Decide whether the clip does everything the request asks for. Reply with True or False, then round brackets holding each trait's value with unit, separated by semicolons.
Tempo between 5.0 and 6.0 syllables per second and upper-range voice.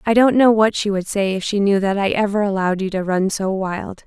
True (5.6 syllables/s; 200 Hz)